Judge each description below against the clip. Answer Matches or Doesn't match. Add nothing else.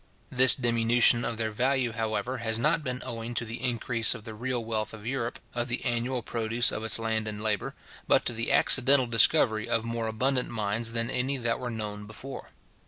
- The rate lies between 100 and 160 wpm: Doesn't match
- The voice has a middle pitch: Doesn't match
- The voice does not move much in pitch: Matches